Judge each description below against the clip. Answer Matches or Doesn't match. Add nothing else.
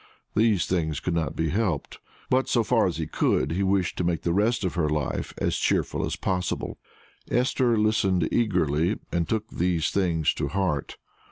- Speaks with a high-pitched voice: Doesn't match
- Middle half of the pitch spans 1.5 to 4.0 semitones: Doesn't match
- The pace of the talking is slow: Doesn't match